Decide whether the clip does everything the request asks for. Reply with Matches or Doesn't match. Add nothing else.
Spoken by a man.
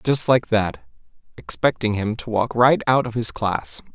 Matches